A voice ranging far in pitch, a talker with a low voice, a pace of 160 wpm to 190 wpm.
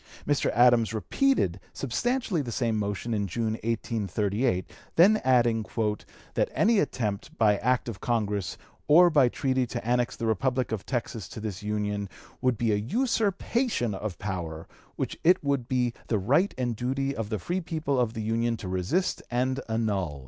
No: average, 4.4 semitones; low, 120 Hz; average, 170 wpm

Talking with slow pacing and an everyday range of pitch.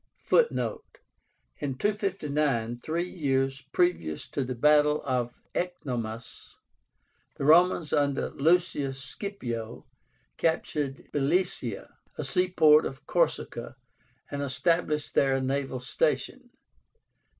Yes: slow, 95 wpm; average, 4.7 semitones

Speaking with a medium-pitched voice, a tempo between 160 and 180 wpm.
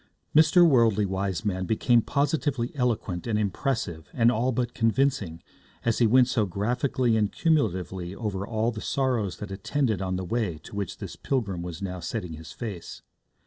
No: low, 110 Hz; average, 165 wpm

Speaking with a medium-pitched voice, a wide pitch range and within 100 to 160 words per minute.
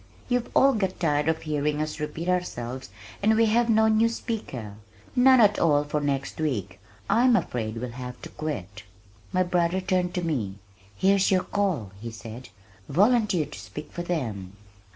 No: medium, 160 Hz; wide, 7.9 semitones; average, 170 wpm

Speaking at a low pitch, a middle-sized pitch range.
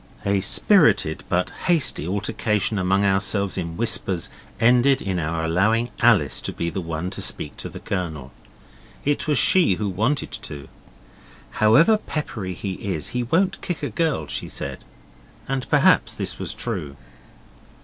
No: low, 100 Hz; wide, 5.8 semitones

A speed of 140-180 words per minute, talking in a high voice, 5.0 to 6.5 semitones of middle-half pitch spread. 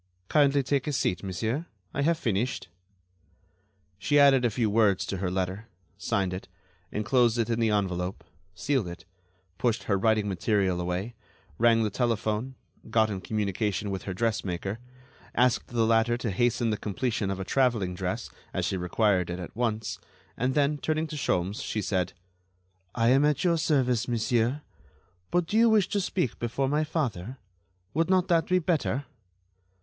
No: average, 165 wpm; low, 115 Hz; wide, 5.6 semitones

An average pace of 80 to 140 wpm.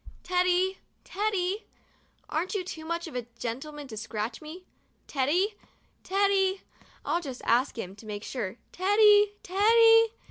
Yes: slow, 135 wpm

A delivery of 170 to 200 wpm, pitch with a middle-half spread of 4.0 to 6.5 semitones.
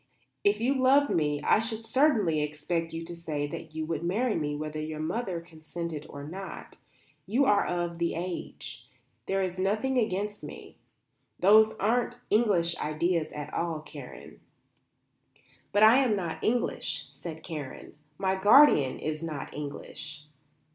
No: average, 145 wpm; wide, 5.6 semitones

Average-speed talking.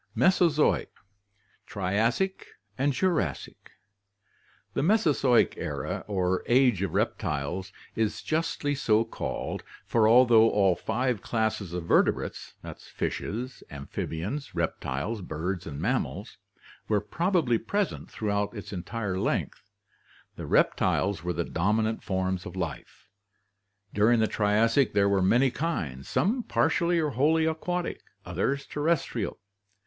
No: slow, 115 wpm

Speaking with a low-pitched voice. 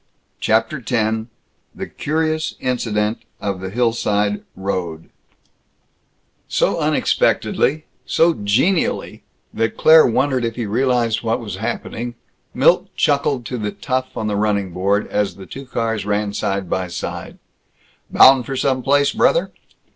Yes: low, 115 Hz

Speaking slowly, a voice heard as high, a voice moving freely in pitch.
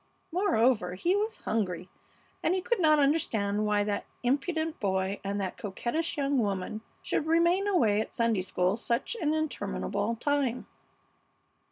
No: average, 145 wpm; high, 235 Hz; wide, 7.8 semitones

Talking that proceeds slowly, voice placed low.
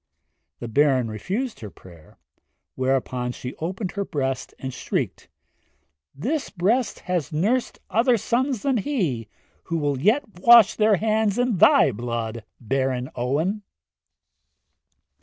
No: slow, 120 wpm; medium, 170 Hz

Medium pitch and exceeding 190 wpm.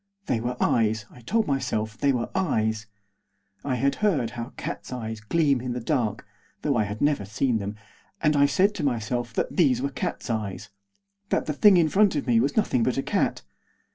No: low, 125 Hz; average, 200 wpm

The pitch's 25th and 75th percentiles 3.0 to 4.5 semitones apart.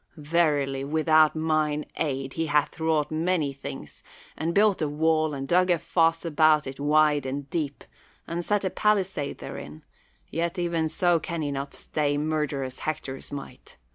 No: narrow, 2.5 semitones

